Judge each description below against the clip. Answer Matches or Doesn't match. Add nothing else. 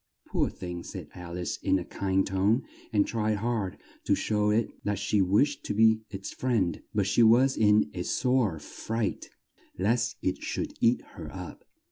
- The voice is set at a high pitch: Doesn't match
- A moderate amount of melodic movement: Matches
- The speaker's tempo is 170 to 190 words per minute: Matches